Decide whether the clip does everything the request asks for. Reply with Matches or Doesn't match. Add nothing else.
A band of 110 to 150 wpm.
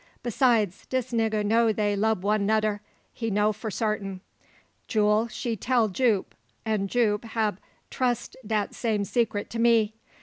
Matches